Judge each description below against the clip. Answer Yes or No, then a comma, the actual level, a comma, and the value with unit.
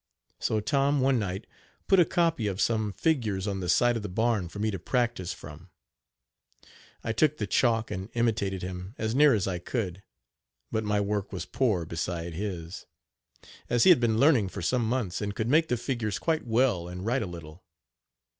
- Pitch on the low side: Yes, low, 110 Hz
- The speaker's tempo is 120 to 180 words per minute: No, average, 190 wpm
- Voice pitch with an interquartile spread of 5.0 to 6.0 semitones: No, average, 4.5 semitones